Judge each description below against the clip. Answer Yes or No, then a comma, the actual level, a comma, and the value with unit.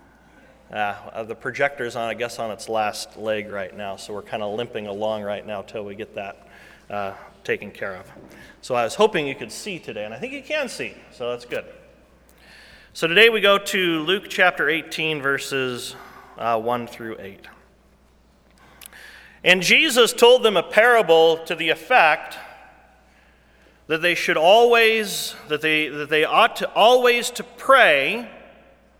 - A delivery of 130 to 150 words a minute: No, average, 165 wpm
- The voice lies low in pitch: No, medium, 155 Hz